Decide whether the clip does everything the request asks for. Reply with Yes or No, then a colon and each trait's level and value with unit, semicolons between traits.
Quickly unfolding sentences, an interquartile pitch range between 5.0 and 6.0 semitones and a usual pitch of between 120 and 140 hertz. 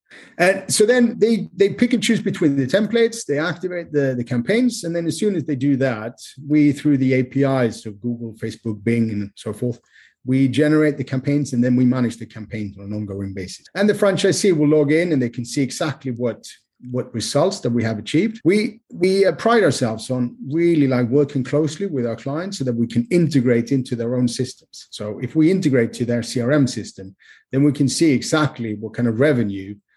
Yes: fast, 210 wpm; wide, 5.6 semitones; low, 135 Hz